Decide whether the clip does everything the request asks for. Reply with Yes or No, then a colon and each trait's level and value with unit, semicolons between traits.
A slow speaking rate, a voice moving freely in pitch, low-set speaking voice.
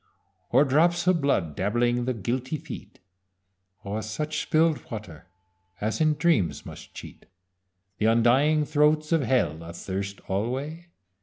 Yes: slow, 130 wpm; wide, 6.4 semitones; low, 130 Hz